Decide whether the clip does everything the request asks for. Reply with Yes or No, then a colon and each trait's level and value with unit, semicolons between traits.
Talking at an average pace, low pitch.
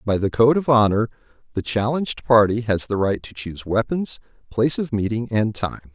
Yes: average, 190 wpm; low, 115 Hz